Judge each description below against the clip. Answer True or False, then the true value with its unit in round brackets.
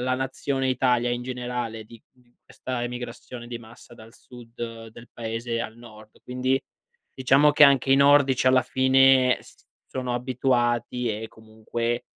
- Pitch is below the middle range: True (125 Hz)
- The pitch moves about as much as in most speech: False (1.9 semitones)